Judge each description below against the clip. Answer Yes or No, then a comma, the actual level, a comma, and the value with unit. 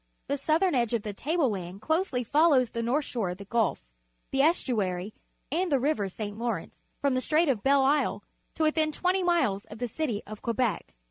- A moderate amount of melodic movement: No, wide, 6.5 semitones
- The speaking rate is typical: No, fast, 210 wpm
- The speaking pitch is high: Yes, very high, 255 Hz